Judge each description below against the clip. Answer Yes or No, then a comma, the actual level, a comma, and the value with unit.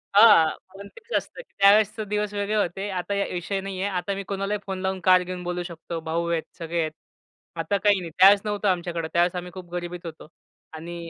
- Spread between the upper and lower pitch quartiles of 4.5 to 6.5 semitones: No, average, 2.7 semitones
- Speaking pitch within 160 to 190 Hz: Yes, medium, 185 Hz